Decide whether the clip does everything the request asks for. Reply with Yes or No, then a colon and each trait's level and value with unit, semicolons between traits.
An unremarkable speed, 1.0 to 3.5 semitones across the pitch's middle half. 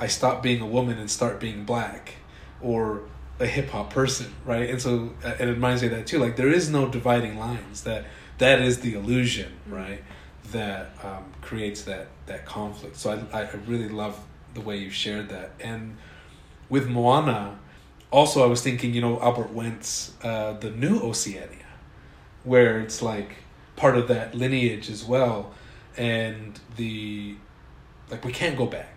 Yes: average, 170 wpm; average, 2.9 semitones